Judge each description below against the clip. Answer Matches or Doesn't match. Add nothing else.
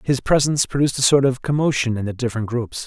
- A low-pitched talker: Matches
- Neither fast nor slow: Doesn't match